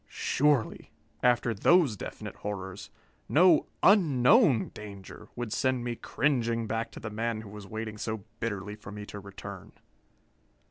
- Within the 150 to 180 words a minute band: No, average, 140 wpm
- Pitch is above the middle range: No, low, 115 Hz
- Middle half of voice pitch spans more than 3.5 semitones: No, average, 3.1 semitones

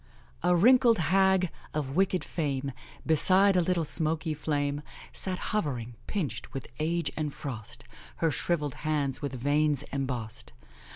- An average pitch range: Yes, average, 4.3 semitones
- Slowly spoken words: Yes, slow, 130 wpm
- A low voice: No, medium, 155 Hz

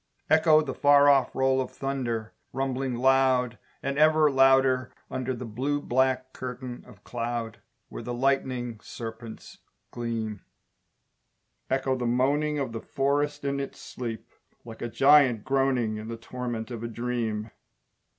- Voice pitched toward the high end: No, low, 130 Hz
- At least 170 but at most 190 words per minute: No, average, 140 wpm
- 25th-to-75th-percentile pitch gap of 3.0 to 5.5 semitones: No, narrow, 2.5 semitones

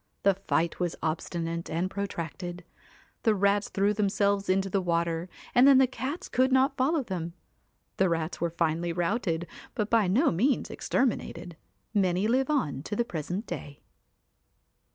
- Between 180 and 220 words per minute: No, average, 155 wpm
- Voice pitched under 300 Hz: Yes, high, 190 Hz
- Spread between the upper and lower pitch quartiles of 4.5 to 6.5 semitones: Yes, average, 5.3 semitones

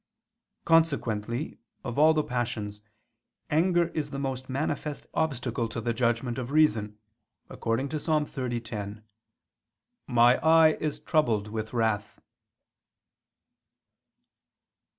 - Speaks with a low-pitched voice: Yes, low, 125 Hz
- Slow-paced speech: Yes, slow, 105 wpm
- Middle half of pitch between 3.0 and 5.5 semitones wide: Yes, average, 5.0 semitones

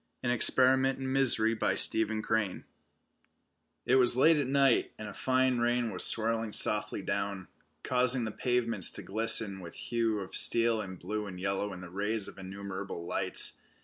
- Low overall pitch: Yes, low, 110 Hz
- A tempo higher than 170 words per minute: No, average, 160 wpm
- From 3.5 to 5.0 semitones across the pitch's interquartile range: Yes, average, 3.8 semitones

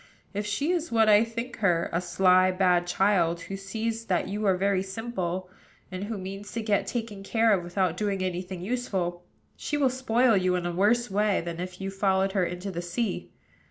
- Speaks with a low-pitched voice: No, high, 195 Hz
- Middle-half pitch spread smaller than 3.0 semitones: No, average, 3.4 semitones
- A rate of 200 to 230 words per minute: Yes, fast, 205 wpm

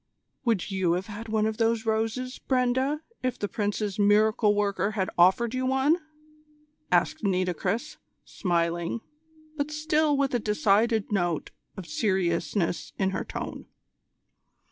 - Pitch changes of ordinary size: Yes, average, 4.6 semitones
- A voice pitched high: Yes, high, 215 Hz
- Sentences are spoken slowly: Yes, slow, 130 wpm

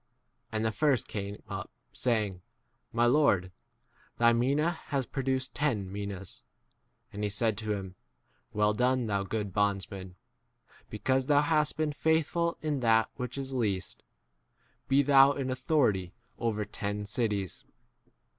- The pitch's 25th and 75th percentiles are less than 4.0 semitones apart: No, average, 5.0 semitones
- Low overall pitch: Yes, low, 115 Hz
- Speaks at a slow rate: No, average, 145 wpm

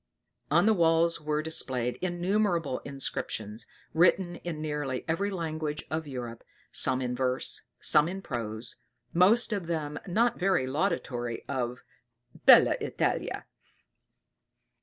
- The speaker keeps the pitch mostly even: No, average, 5.2 semitones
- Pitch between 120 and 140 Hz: No, medium, 155 Hz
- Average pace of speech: No, slow, 115 wpm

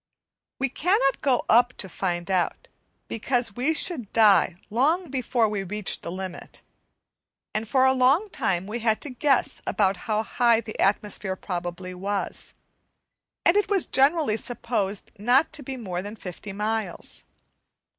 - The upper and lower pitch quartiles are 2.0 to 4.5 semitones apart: No, average, 5.2 semitones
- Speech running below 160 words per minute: Yes, average, 150 wpm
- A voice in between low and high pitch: No, high, 225 Hz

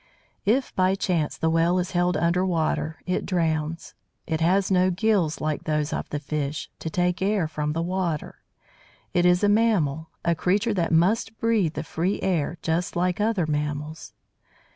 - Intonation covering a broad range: No, average, 3.0 semitones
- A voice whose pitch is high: No, medium, 175 Hz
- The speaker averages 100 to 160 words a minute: No, average, 170 wpm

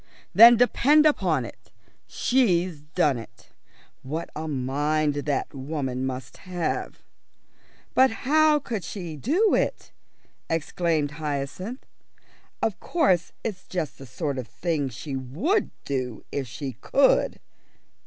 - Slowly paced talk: Yes, slow, 120 wpm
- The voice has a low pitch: No, medium, 160 Hz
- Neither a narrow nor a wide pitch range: No, wide, 8.1 semitones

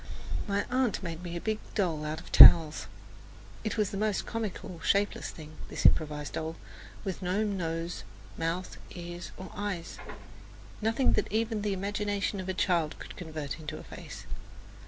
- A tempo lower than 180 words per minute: Yes, average, 160 wpm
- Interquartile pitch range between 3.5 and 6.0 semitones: Yes, average, 3.9 semitones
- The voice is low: No, medium, 185 Hz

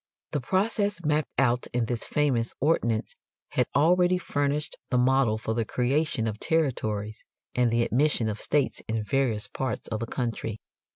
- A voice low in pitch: Yes, low, 125 Hz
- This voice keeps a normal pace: Yes, average, 160 wpm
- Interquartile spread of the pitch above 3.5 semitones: Yes, average, 4.8 semitones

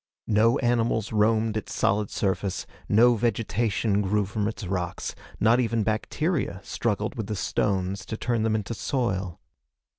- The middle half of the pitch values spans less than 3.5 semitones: Yes, narrow, 2.6 semitones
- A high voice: No, low, 110 Hz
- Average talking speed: Yes, average, 145 wpm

